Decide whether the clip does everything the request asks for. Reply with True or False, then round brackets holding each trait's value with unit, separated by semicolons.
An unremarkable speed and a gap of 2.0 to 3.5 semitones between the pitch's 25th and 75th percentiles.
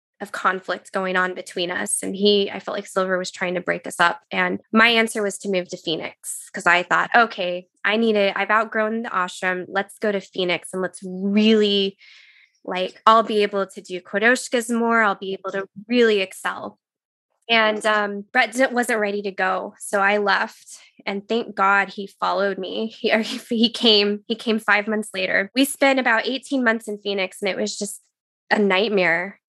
True (195 wpm; 2.9 semitones)